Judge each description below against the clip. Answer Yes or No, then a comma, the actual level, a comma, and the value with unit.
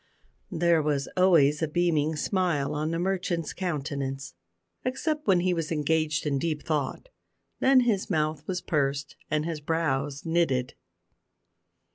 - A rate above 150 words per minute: No, slow, 135 wpm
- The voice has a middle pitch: Yes, medium, 160 Hz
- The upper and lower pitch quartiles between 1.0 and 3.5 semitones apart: Yes, average, 3.2 semitones